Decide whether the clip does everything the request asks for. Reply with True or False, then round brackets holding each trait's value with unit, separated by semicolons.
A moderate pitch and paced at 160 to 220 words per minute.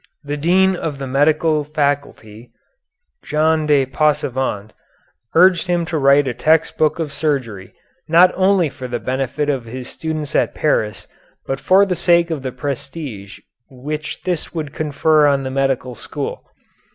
False (145 Hz; 150 wpm)